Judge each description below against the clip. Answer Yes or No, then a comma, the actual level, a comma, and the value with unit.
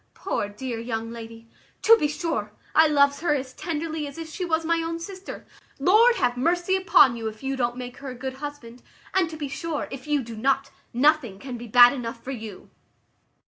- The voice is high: Yes, very high, 275 Hz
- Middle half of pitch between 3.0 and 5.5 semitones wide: Yes, average, 5.1 semitones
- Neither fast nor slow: No, fast, 210 wpm